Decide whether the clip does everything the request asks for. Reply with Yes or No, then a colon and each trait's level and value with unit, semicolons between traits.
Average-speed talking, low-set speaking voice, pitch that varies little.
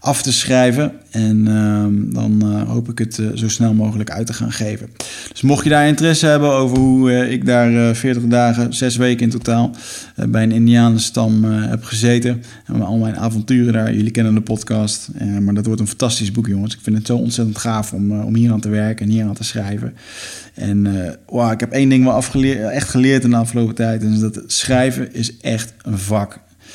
No: fast, 230 wpm; low, 115 Hz; narrow, 2.2 semitones